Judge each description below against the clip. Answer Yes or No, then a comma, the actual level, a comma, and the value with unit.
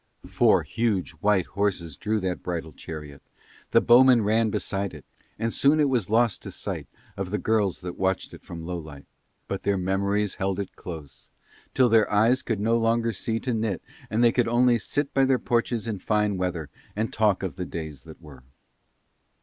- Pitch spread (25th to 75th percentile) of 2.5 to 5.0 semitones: Yes, average, 4.2 semitones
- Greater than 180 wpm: Yes, average, 190 wpm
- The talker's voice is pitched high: No, low, 105 Hz